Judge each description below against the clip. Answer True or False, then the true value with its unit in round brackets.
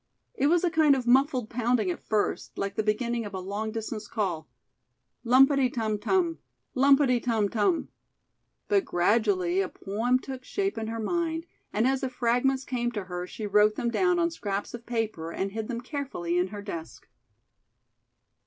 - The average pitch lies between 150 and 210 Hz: False (230 Hz)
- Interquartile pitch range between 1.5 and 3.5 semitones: False (4.6 semitones)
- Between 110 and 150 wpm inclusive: False (175 wpm)